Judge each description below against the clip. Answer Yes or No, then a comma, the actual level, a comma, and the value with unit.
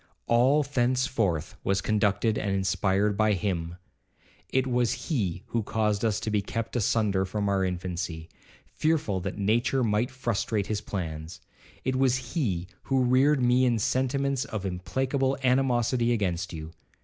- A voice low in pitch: Yes, low, 110 Hz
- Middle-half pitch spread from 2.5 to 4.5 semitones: No, average, 4.9 semitones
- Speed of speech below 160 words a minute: Yes, average, 140 wpm